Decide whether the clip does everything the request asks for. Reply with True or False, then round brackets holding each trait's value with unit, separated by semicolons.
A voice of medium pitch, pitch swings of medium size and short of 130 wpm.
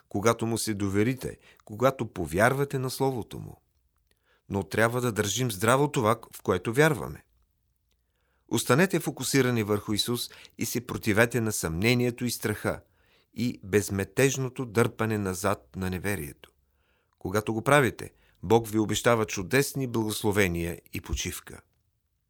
False (110 Hz; 3.4 semitones; 120 wpm)